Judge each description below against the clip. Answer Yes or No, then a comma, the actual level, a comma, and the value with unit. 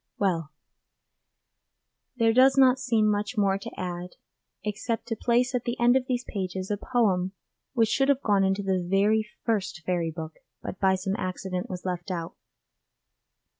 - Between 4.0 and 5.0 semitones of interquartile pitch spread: Yes, average, 4.4 semitones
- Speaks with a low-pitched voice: No, high, 200 Hz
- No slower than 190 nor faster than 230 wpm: No, average, 165 wpm